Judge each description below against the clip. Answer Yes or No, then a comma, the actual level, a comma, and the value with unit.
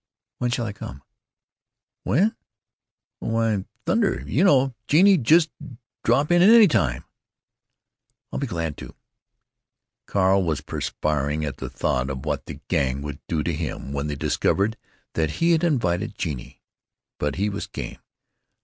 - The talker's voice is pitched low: Yes, low, 100 Hz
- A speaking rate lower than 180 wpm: Yes, average, 140 wpm